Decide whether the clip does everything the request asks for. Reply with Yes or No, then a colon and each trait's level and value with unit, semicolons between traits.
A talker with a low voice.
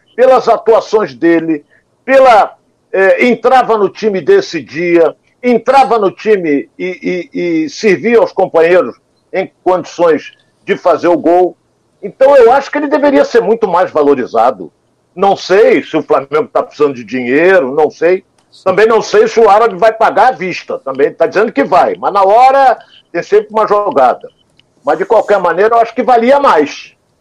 No: high, 215 Hz